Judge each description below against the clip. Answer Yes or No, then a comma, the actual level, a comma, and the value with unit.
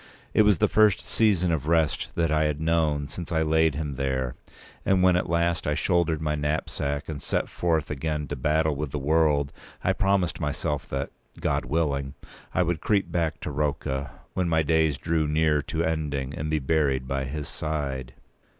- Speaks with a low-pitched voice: Yes, very low, 75 Hz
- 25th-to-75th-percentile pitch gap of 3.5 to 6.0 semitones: No, narrow, 2.4 semitones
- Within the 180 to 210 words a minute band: Yes, average, 190 wpm